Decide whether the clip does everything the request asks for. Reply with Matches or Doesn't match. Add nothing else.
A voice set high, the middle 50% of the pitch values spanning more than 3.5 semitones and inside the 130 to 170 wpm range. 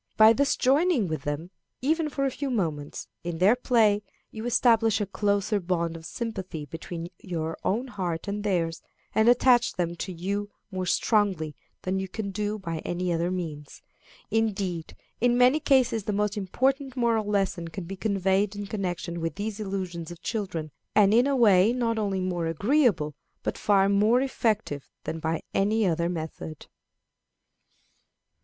Matches